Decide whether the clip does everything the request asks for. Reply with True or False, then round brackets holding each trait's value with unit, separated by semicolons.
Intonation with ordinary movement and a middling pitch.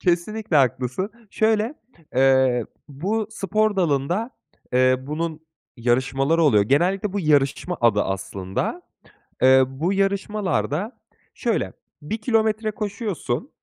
False (7.9 semitones; 170 Hz)